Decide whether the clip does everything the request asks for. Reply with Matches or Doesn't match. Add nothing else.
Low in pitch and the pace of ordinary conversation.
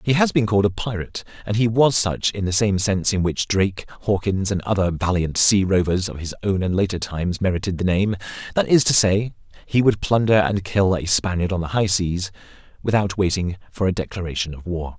Doesn't match